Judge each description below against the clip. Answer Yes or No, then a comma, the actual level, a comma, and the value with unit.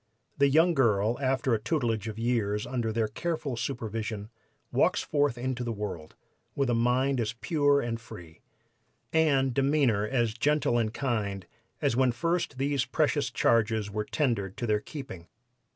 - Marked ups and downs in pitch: No, average, 4.0 semitones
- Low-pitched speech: Yes, low, 120 Hz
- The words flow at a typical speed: Yes, average, 155 wpm